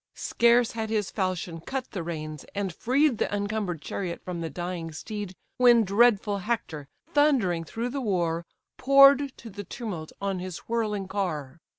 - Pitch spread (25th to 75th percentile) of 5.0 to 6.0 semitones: Yes, average, 5.3 semitones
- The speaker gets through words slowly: No, average, 160 wpm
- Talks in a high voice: Yes, high, 200 Hz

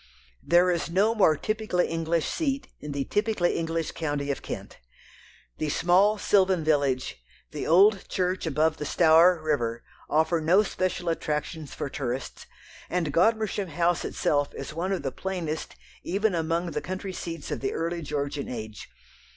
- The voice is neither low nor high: Yes, medium, 165 Hz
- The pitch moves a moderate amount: Yes, average, 3.7 semitones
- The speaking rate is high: No, average, 155 wpm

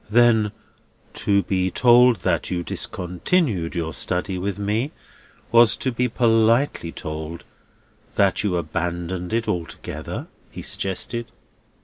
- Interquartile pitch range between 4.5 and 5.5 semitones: Yes, average, 5.0 semitones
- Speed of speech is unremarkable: No, slow, 115 wpm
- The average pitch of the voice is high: No, low, 100 Hz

